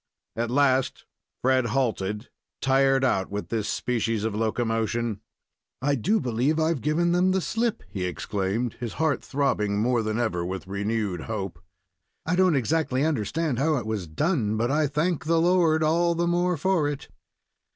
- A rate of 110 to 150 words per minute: No, average, 160 wpm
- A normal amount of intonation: No, wide, 6.6 semitones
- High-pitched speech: No, low, 130 Hz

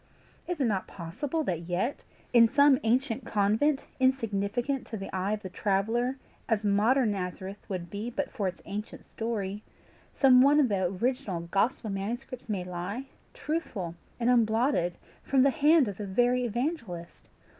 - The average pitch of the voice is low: No, high, 225 Hz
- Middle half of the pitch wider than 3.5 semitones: Yes, average, 5.0 semitones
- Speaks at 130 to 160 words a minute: Yes, average, 155 wpm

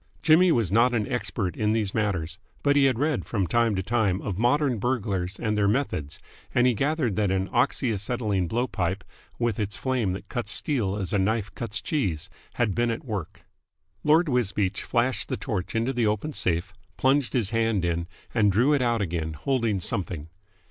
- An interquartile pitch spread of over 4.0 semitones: Yes, average, 4.4 semitones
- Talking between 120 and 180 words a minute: No, average, 190 wpm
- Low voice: Yes, low, 110 Hz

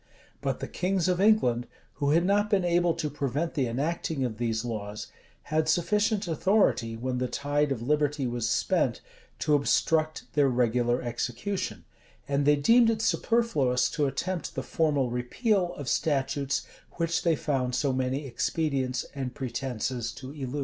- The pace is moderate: Yes, average, 155 wpm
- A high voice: No, medium, 140 Hz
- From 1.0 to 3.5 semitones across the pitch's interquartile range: No, average, 4.9 semitones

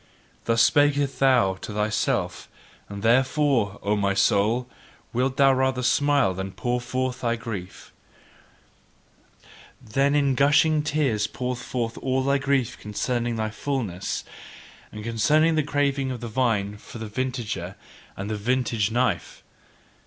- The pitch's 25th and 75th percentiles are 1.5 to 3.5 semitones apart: No, average, 4.1 semitones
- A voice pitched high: No, low, 125 Hz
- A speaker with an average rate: No, slow, 130 wpm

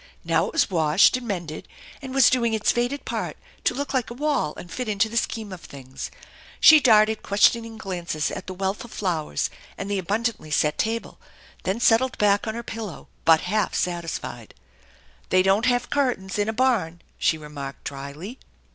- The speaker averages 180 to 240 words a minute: Yes, average, 190 wpm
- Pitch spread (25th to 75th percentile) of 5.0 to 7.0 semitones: Yes, wide, 5.5 semitones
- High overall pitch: Yes, high, 205 Hz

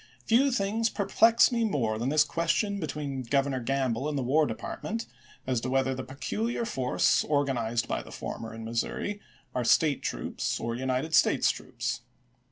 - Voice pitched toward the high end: No, medium, 140 Hz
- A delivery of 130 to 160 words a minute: No, average, 170 wpm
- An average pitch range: No, wide, 7.9 semitones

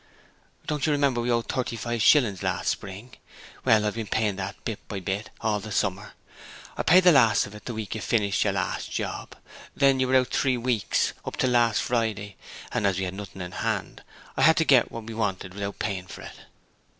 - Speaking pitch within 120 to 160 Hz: No, low, 110 Hz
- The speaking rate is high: Yes, fast, 220 wpm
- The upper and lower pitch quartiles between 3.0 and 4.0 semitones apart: Yes, average, 3.6 semitones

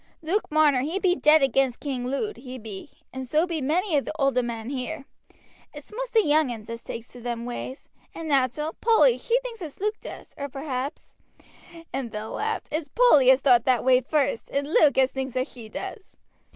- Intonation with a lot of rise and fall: No, average, 4.1 semitones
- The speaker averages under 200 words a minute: No, fast, 205 wpm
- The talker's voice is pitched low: No, very high, 275 Hz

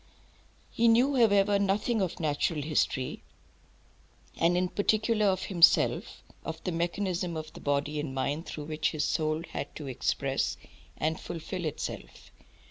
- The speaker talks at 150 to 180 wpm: No, average, 140 wpm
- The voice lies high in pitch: No, medium, 170 Hz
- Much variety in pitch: No, average, 4.5 semitones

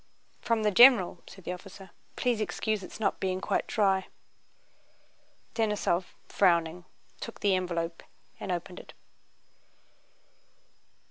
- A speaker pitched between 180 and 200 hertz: Yes, high, 190 Hz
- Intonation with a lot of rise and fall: No, average, 3.0 semitones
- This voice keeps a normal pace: No, slow, 115 wpm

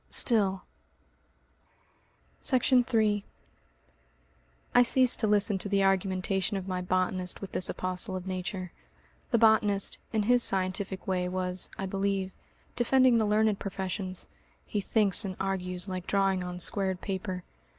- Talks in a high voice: Yes, high, 195 Hz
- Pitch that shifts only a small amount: Yes, narrow, 2.2 semitones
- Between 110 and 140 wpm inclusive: Yes, slow, 135 wpm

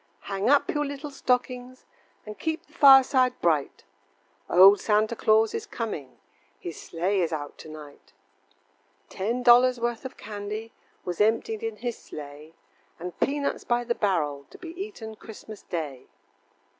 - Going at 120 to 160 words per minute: Yes, average, 145 wpm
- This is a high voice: Yes, high, 220 Hz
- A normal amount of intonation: No, wide, 6.3 semitones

